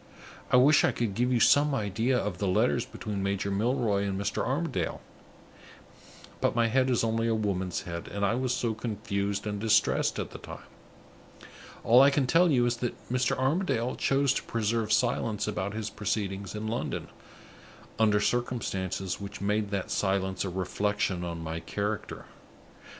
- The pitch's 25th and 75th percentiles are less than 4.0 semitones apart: Yes, average, 3.5 semitones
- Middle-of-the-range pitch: No, low, 105 Hz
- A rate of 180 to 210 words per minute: No, average, 165 wpm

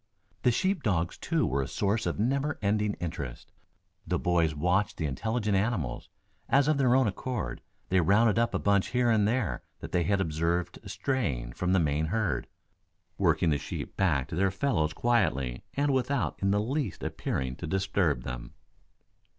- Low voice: Yes, very low, 95 Hz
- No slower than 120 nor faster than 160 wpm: No, average, 175 wpm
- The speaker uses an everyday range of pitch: No, wide, 6.8 semitones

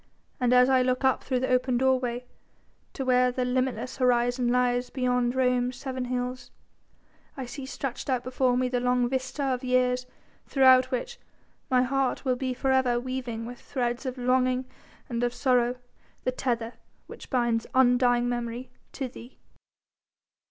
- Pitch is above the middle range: Yes, very high, 250 Hz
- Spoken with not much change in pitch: Yes, narrow, 0.9 semitones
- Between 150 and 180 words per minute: Yes, average, 160 wpm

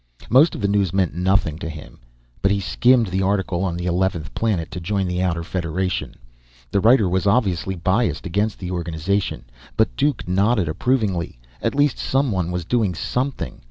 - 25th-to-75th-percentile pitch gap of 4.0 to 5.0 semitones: No, average, 3.2 semitones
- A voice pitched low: Yes, very low, 95 Hz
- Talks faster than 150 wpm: Yes, average, 175 wpm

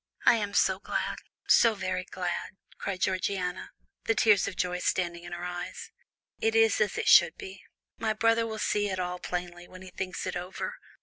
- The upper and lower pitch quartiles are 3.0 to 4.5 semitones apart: No, narrow, 2.6 semitones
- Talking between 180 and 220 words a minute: Yes, average, 190 wpm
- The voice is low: No, medium, 185 Hz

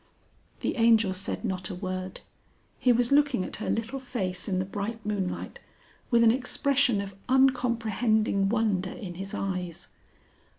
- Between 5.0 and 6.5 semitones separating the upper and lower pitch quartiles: No, average, 4.3 semitones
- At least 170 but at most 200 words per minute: No, average, 145 wpm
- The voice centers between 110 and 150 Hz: No, high, 215 Hz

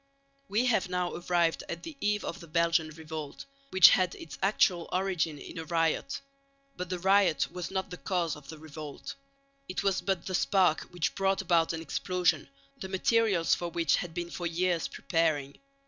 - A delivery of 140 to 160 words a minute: No, average, 180 wpm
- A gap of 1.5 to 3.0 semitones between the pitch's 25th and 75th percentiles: Yes, narrow, 2.6 semitones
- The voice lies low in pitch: No, medium, 175 Hz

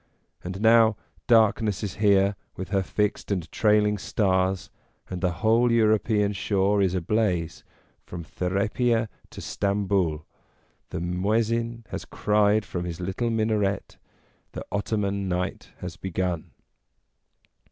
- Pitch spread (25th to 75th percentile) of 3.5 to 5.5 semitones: No, average, 2.8 semitones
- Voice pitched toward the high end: No, low, 100 Hz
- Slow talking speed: Yes, slow, 120 wpm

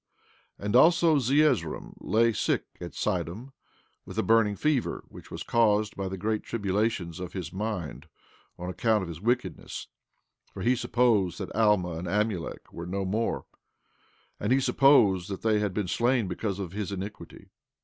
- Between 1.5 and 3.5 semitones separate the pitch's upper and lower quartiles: No, average, 3.9 semitones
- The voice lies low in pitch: Yes, low, 105 Hz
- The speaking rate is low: No, average, 165 wpm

